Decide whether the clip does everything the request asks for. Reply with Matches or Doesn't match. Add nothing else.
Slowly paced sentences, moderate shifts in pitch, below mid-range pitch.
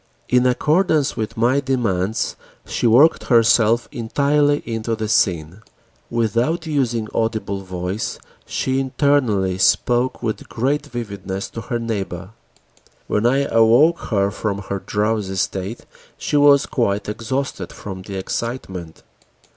Matches